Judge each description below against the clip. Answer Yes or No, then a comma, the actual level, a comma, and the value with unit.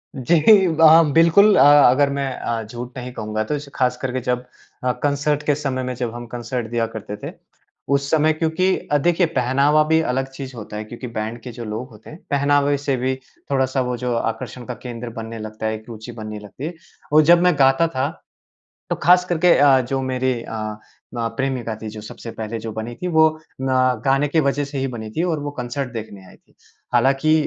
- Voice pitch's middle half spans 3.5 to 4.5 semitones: Yes, average, 3.9 semitones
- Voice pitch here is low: Yes, low, 130 Hz